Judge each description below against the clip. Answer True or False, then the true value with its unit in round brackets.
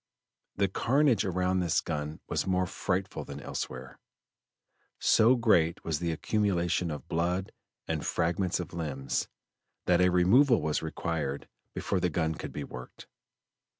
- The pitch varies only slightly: False (3.0 semitones)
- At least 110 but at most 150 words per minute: True (140 wpm)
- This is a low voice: True (90 Hz)